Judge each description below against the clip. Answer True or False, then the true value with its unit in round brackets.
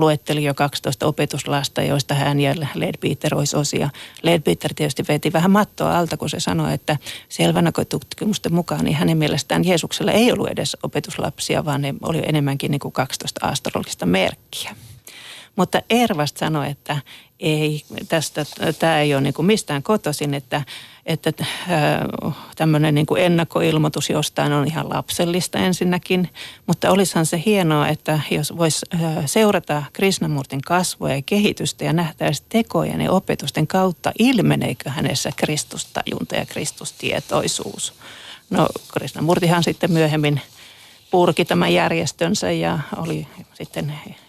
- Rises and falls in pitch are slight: False (3.3 semitones)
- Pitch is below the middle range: False (155 Hz)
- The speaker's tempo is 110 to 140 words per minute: True (130 wpm)